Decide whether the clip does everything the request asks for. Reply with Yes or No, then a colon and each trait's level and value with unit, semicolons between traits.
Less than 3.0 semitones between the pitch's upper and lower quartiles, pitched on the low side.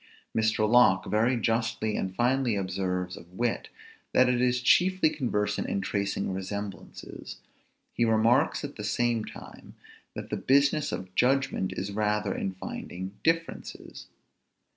No: average, 4.2 semitones; low, 110 Hz